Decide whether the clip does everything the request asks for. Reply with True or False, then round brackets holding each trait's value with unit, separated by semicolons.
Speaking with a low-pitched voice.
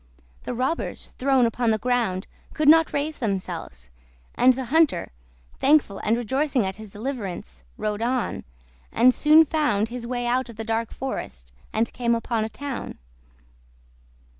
False (240 Hz)